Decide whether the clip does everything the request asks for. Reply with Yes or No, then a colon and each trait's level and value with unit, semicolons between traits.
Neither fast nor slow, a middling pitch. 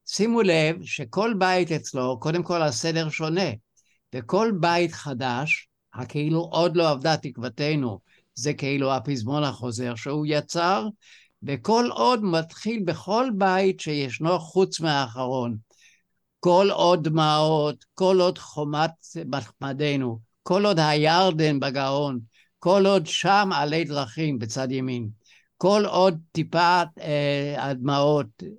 Yes: average, 110 wpm; medium, 155 Hz